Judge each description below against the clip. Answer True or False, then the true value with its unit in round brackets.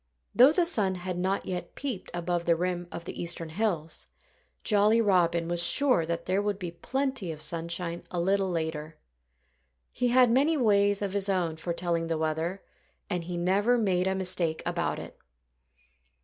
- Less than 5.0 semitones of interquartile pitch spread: True (3.3 semitones)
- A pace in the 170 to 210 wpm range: True (175 wpm)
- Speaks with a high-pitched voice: False (180 Hz)